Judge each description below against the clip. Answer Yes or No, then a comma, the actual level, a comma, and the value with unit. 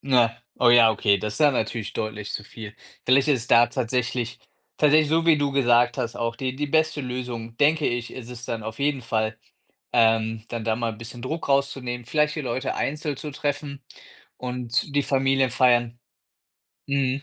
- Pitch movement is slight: No, average, 3.2 semitones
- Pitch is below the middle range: Yes, low, 125 Hz